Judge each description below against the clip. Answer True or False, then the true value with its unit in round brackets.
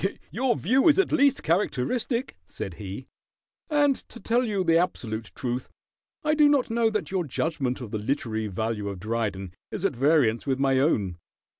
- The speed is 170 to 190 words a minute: True (175 wpm)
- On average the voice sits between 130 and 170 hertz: True (140 Hz)